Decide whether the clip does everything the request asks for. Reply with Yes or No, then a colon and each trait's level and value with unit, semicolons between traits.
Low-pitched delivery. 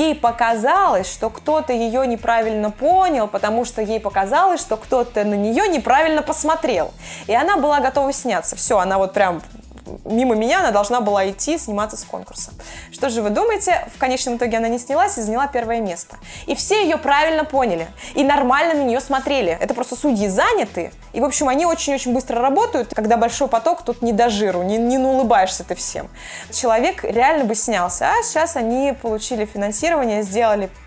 No: high, 245 Hz